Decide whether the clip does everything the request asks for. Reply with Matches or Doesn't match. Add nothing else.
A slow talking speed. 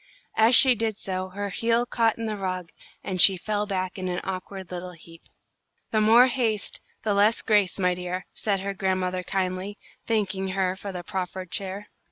Doesn't match